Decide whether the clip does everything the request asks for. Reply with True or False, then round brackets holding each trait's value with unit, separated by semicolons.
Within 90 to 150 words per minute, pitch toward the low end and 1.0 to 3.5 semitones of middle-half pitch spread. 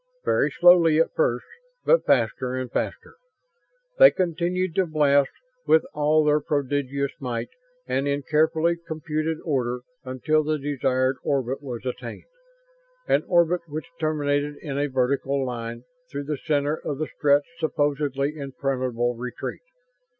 False (135 wpm; 145 Hz; 3.0 semitones)